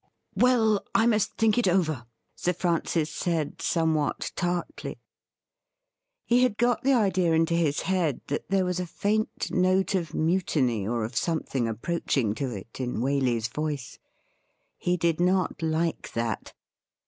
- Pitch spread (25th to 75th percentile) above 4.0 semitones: Yes, average, 5.1 semitones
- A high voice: No, medium, 170 Hz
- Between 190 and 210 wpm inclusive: No, average, 150 wpm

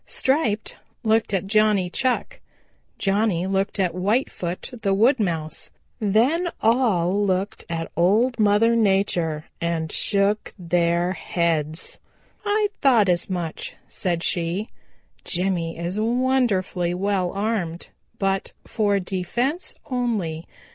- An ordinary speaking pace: No, slow, 110 wpm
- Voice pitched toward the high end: Yes, high, 195 Hz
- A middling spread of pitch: Yes, average, 4.3 semitones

